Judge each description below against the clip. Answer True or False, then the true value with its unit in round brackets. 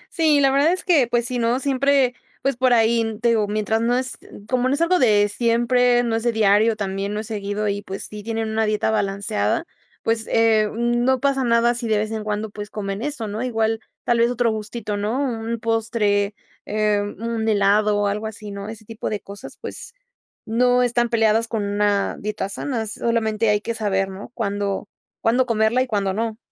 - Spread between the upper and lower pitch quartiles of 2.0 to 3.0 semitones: True (2.5 semitones)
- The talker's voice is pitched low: False (225 Hz)